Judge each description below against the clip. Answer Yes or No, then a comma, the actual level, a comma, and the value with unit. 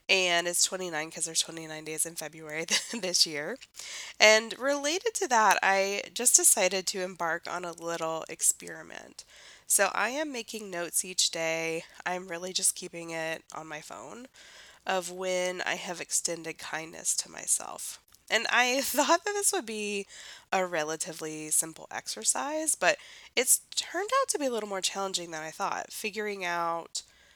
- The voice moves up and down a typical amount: No, wide, 5.9 semitones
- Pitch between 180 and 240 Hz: Yes, medium, 185 Hz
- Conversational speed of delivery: Yes, average, 160 wpm